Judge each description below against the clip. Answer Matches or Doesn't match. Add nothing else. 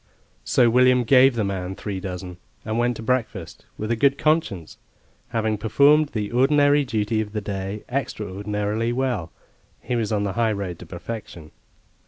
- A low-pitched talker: Matches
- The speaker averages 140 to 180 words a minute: Matches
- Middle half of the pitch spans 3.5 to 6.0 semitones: Matches